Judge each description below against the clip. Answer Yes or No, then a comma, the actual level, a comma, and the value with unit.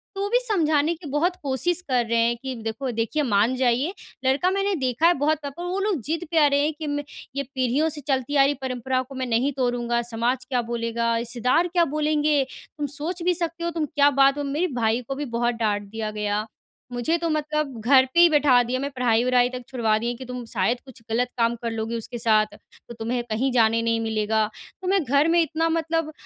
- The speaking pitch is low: No, very high, 260 Hz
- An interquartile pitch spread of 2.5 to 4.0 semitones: No, average, 4.6 semitones